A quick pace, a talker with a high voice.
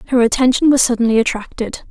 No: average, 155 wpm; high, 240 Hz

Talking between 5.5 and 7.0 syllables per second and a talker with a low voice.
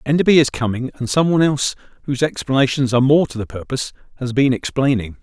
Yes: 6.9 syllables/s; low, 130 Hz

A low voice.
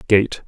Yes: low, 105 Hz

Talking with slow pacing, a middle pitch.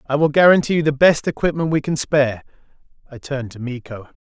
No: average, 200 wpm; medium, 145 Hz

